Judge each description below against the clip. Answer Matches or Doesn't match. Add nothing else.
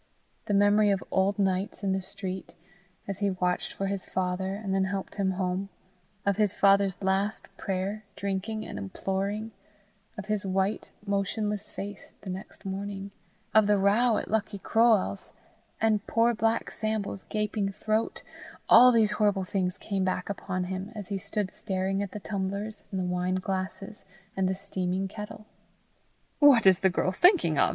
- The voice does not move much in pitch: Matches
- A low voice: Doesn't match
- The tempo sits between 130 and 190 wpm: Matches